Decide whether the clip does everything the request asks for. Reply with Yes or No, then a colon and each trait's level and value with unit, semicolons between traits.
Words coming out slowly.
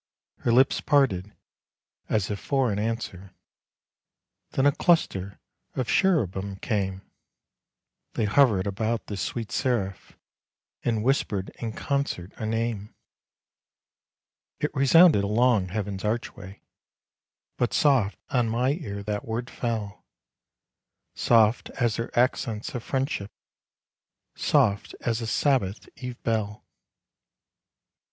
Yes: slow, 110 wpm